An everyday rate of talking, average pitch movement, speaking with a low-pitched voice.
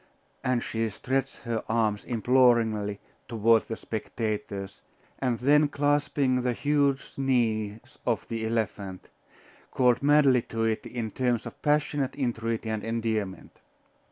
No: slow, 125 wpm; average, 3.1 semitones; low, 115 Hz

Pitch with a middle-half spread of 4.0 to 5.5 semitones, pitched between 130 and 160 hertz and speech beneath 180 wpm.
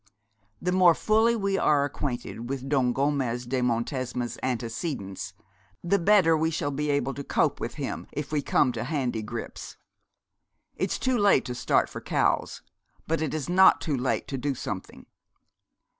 Yes: average, 4.8 semitones; medium, 140 Hz; average, 165 wpm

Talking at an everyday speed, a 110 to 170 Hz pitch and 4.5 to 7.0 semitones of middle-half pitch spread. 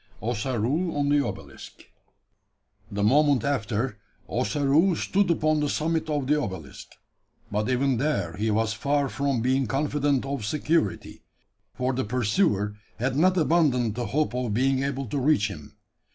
Yes: average, 150 wpm; low, 135 Hz; average, 4.8 semitones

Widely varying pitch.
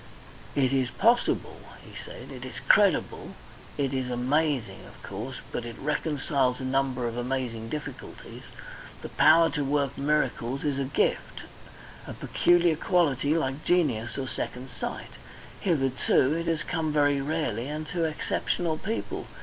No: average, 3.5 semitones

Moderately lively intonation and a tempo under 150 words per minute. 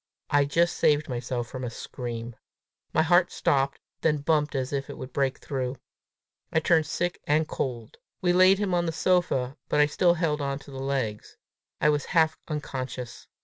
No: average, 3.8 semitones; average, 185 wpm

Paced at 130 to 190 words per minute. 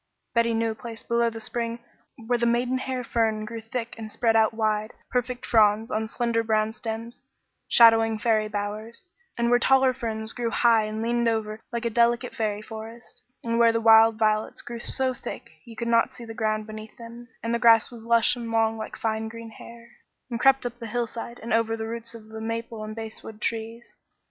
No: average, 200 wpm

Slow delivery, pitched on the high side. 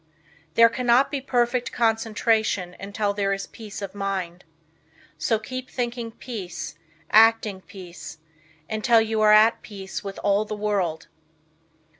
Yes: slow, 130 wpm; high, 215 Hz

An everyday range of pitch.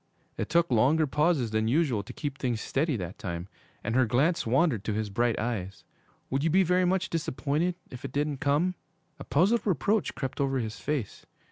No: wide, 6.1 semitones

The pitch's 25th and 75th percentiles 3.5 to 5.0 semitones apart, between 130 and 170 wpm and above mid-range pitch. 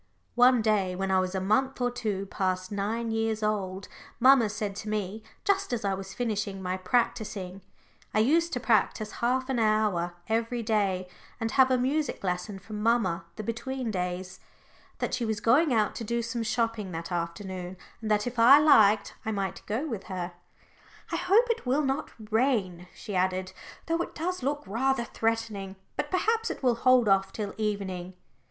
No: average, 4.3 semitones; average, 185 wpm; high, 215 Hz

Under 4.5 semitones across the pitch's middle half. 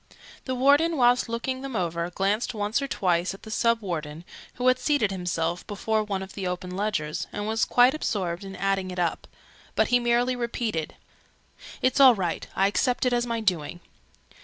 No: average, 5.3 semitones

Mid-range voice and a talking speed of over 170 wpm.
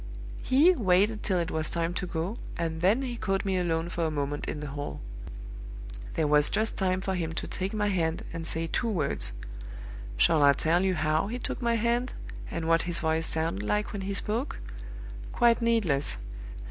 Yes: medium, 175 Hz; average, 195 wpm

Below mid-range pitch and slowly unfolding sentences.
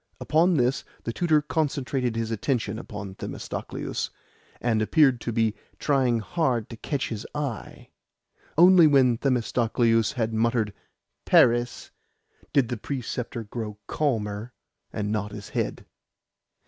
Yes: low, 120 Hz; slow, 120 wpm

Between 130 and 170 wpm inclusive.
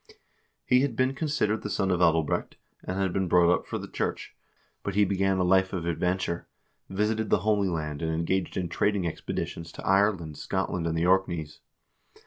No: average, 190 wpm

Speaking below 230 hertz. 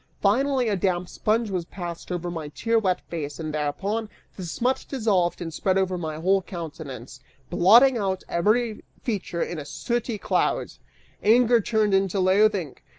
Yes: high, 190 Hz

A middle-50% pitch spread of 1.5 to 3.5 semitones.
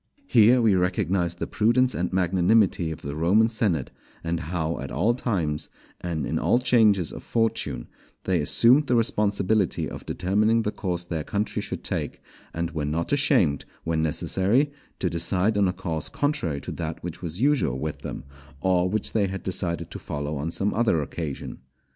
No: average, 5.0 semitones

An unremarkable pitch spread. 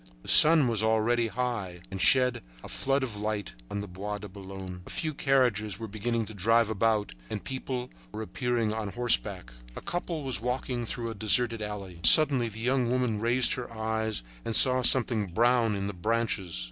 Yes: average, 3.2 semitones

